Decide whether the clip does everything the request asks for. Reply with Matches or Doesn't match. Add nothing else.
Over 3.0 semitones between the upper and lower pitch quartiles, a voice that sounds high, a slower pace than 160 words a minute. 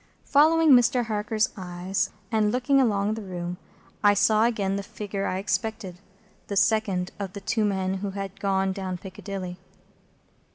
Doesn't match